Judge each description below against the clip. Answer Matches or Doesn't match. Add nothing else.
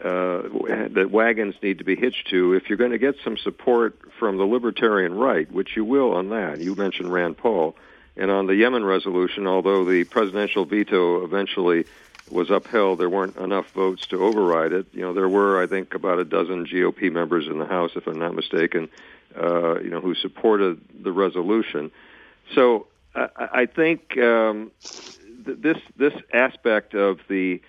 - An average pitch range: Matches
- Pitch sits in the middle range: Doesn't match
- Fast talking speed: Doesn't match